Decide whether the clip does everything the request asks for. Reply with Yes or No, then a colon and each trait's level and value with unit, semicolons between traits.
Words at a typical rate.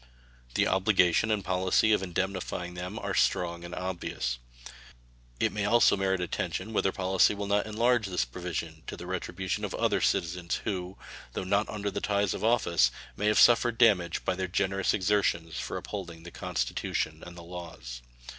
Yes: average, 170 wpm